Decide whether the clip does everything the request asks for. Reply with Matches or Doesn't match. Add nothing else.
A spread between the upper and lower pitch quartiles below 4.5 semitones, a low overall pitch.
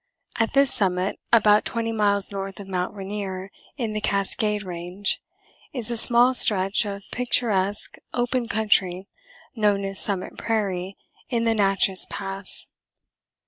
Doesn't match